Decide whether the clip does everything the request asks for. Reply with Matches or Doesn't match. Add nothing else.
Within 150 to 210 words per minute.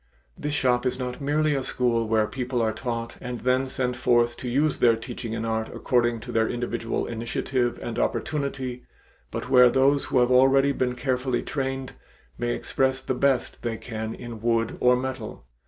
Matches